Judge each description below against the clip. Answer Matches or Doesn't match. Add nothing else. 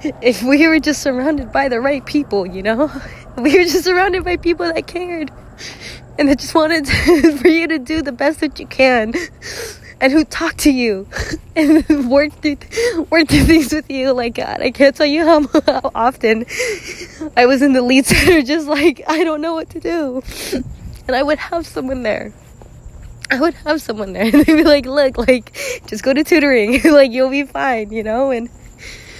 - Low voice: Doesn't match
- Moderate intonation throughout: Matches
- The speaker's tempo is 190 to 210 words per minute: Matches